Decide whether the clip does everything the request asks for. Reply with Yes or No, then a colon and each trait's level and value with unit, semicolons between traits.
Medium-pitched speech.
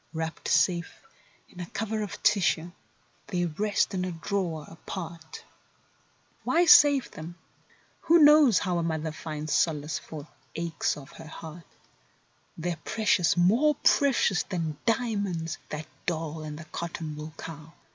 Yes: medium, 170 Hz